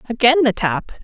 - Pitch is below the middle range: No, high, 215 Hz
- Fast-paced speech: No, average, 175 wpm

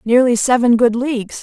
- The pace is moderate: Yes, average, 170 wpm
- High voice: Yes, high, 240 Hz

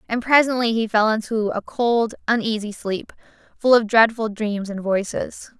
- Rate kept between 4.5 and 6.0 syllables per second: Yes, 4.6 syllables/s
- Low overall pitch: No, high, 220 Hz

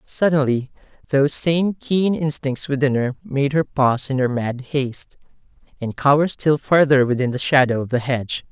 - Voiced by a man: Yes, male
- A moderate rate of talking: Yes, average, 170 wpm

